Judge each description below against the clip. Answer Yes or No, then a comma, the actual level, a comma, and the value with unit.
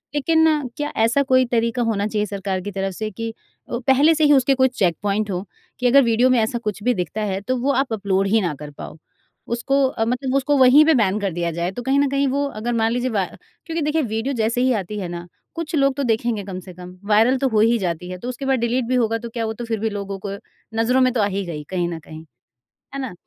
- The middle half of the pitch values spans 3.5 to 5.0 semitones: Yes, average, 4.7 semitones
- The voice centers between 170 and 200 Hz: No, high, 230 Hz